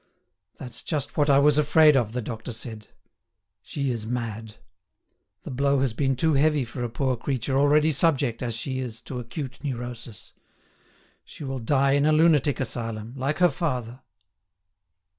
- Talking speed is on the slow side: No, average, 160 wpm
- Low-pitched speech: Yes, low, 130 Hz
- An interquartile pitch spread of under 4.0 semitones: Yes, average, 3.4 semitones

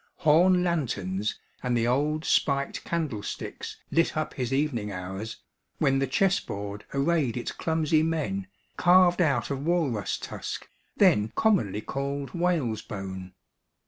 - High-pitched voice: No, medium, 140 Hz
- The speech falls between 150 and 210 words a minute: No, slow, 135 wpm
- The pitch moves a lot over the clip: Yes, wide, 7.4 semitones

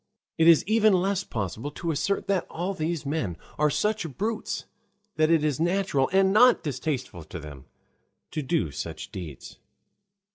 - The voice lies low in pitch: No, medium, 160 Hz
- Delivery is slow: No, average, 155 wpm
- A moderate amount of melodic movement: No, wide, 6.8 semitones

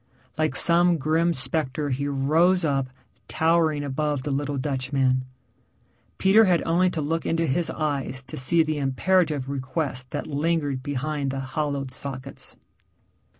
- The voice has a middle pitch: Yes, medium, 145 Hz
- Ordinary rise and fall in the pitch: Yes, average, 3.4 semitones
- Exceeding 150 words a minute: No, average, 140 wpm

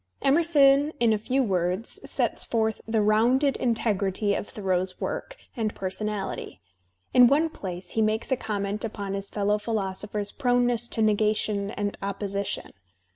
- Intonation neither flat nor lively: Yes, average, 3.1 semitones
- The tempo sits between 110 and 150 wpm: Yes, average, 140 wpm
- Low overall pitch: No, high, 215 Hz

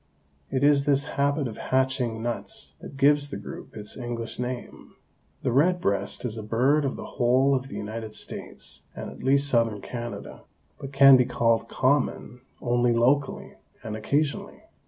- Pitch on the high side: No, low, 125 Hz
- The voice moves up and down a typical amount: Yes, average, 3.2 semitones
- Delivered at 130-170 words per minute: Yes, average, 165 wpm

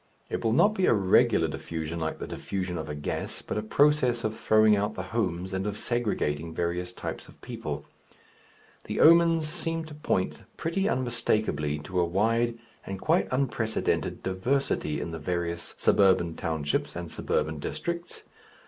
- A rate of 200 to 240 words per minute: No, average, 160 wpm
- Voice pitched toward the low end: Yes, low, 105 Hz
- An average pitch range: No, wide, 6.9 semitones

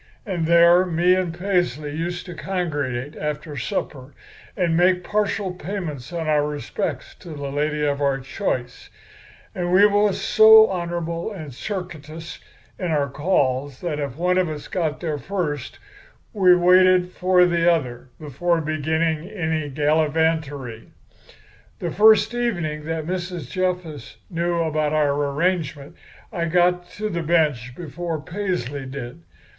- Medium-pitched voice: Yes, medium, 165 Hz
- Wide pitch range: No, average, 3.5 semitones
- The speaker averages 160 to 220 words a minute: No, average, 140 wpm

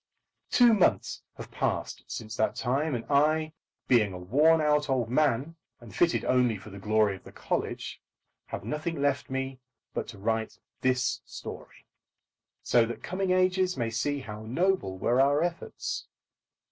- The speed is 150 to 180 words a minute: Yes, average, 160 wpm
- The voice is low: Yes, low, 130 Hz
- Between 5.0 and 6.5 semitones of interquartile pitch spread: Yes, wide, 5.6 semitones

